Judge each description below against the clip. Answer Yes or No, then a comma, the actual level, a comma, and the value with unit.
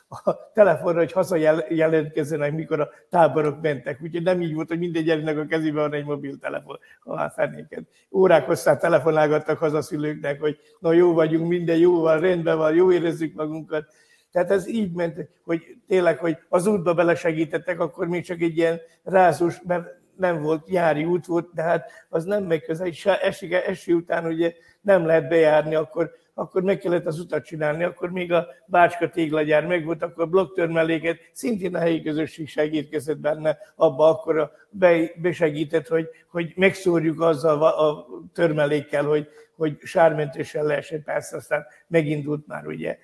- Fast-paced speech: Yes, fast, 165 wpm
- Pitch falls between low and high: Yes, medium, 165 Hz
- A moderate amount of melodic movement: No, narrow, 2.1 semitones